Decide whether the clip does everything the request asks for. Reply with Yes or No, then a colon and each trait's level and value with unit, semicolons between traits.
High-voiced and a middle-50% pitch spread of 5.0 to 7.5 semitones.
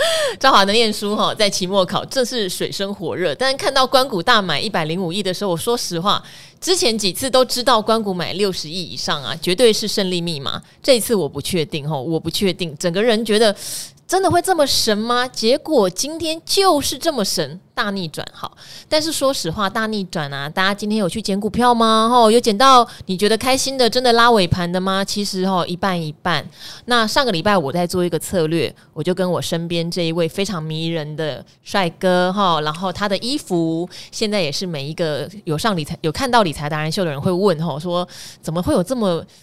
Yes: high, 195 Hz; average, 5.3 semitones